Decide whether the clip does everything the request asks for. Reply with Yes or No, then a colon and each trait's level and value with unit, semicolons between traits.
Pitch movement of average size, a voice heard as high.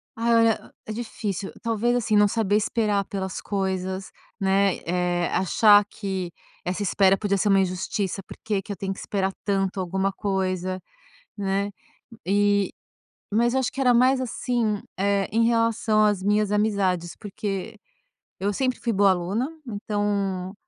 No: narrow, 2.0 semitones; high, 200 Hz